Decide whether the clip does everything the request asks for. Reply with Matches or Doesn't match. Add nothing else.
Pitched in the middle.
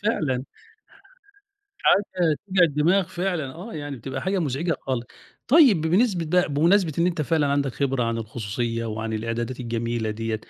Matches